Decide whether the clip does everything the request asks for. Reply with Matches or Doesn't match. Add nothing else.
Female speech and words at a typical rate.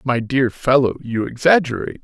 Doesn't match